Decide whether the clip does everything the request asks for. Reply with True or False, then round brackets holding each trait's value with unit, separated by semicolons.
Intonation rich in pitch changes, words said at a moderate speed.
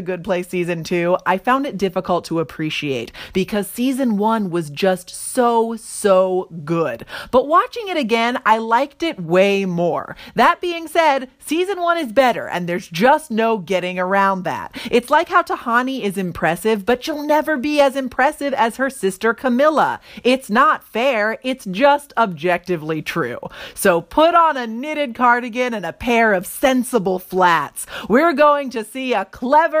True (7.1 semitones; 165 wpm)